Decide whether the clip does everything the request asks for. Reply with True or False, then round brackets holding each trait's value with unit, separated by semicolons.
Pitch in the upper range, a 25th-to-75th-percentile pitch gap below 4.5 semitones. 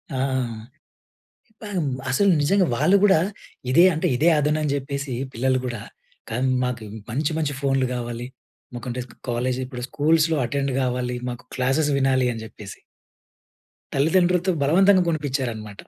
False (135 Hz; 4.1 semitones)